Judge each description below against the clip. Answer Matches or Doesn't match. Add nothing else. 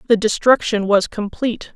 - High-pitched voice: Matches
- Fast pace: Doesn't match